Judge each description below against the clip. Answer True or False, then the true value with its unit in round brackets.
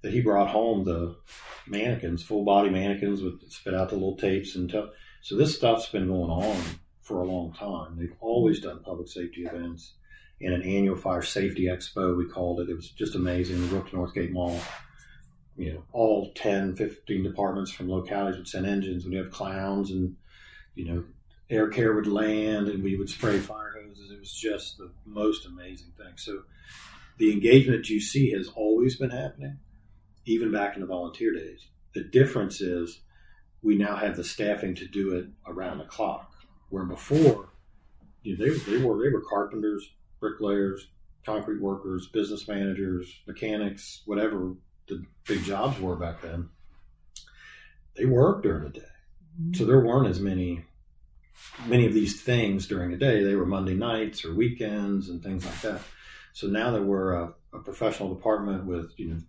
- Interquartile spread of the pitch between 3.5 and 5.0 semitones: False (3.0 semitones)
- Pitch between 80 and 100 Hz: True (95 Hz)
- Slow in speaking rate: False (175 wpm)